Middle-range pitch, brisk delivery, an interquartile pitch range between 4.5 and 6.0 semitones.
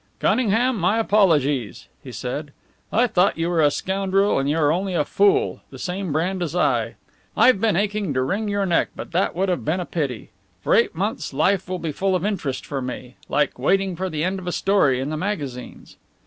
Yes: medium, 180 Hz; fast, 215 wpm; average, 5.1 semitones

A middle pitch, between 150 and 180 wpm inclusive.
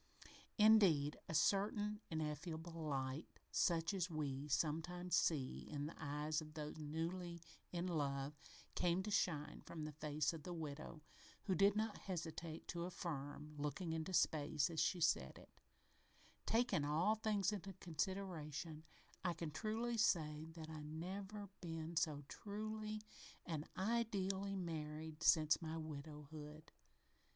No: medium, 165 Hz; average, 140 wpm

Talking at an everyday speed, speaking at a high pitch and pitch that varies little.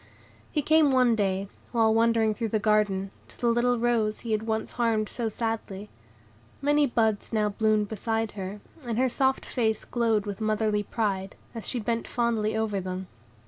Yes: average, 175 wpm; high, 220 Hz; narrow, 2.1 semitones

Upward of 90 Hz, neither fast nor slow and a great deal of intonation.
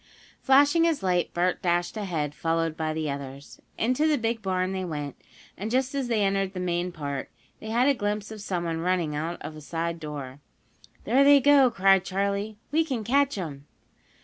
Yes: high, 190 Hz; average, 190 wpm; wide, 6.0 semitones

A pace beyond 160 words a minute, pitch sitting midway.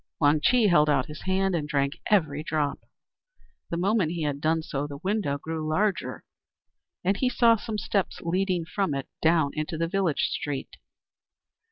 Yes: average, 170 wpm; medium, 165 Hz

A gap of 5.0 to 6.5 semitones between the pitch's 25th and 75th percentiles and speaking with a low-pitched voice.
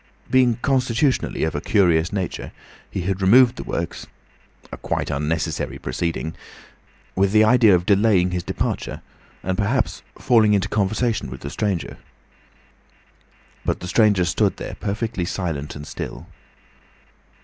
No: average, 4.3 semitones; very low, 95 Hz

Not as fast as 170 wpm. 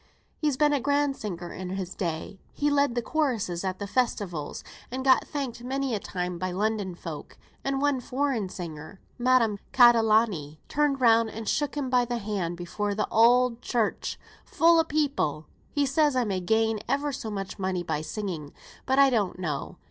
No: average, 180 wpm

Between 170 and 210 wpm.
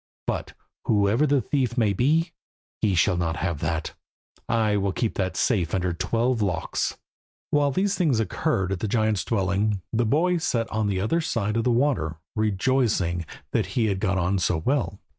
Yes: average, 180 wpm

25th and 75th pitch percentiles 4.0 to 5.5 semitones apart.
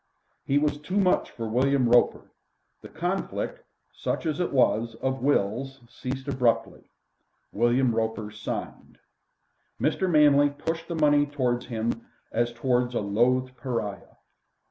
No: average, 3.6 semitones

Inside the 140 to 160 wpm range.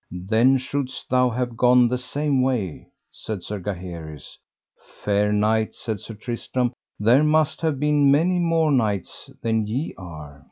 Yes: average, 150 wpm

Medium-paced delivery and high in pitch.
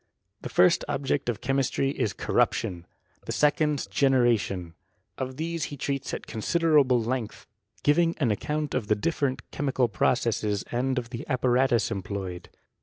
No: average, 145 wpm; low, 130 Hz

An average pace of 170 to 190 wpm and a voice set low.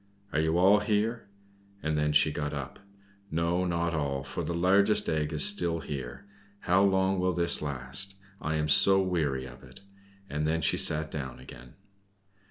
Yes: average, 175 wpm; very low, 80 Hz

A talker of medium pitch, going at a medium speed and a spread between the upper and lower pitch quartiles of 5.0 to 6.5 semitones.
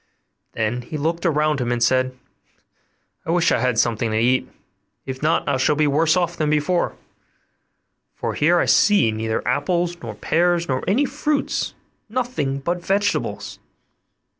Yes: medium, 150 Hz; average, 165 wpm; wide, 5.4 semitones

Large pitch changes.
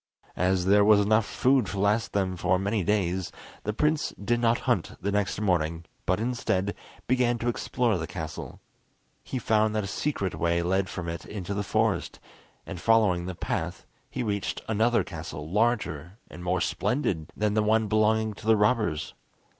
No: average, 3.4 semitones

